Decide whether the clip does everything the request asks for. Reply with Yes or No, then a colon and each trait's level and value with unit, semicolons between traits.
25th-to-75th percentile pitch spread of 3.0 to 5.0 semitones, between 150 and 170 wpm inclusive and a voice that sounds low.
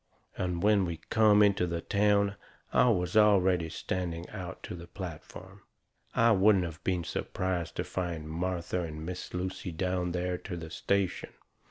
No: narrow, 2.5 semitones; average, 160 wpm; very low, 90 Hz